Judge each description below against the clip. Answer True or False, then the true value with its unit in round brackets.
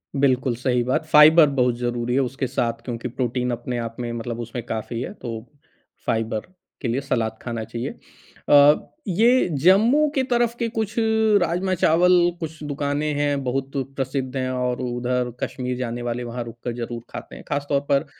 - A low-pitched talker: True (125 Hz)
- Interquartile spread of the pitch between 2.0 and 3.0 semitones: False (3.5 semitones)